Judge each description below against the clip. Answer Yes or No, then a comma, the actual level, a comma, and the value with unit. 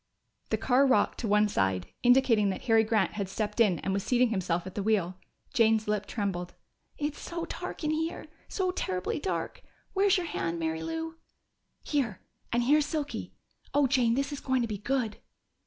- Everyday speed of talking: Yes, average, 185 wpm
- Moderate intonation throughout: No, wide, 6.1 semitones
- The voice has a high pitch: Yes, high, 230 Hz